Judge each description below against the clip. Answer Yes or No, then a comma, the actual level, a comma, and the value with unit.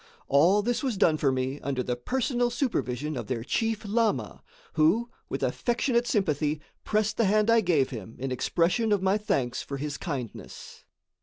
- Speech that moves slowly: No, average, 170 wpm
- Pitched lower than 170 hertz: No, medium, 175 Hz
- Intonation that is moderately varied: No, wide, 8.6 semitones